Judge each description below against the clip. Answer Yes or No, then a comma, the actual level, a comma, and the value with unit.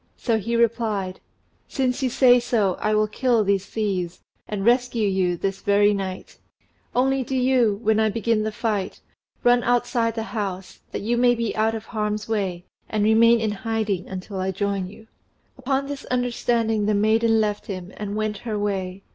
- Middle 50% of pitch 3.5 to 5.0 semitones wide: No, average, 2.8 semitones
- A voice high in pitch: Yes, high, 215 Hz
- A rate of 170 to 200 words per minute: Yes, average, 180 wpm